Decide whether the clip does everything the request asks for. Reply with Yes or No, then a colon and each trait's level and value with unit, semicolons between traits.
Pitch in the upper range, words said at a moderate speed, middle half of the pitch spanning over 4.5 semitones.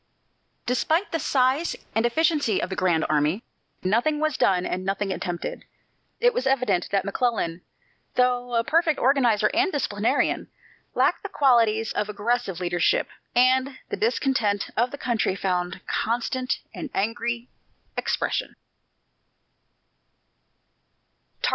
No: high, 235 Hz; slow, 120 wpm; average, 5.1 semitones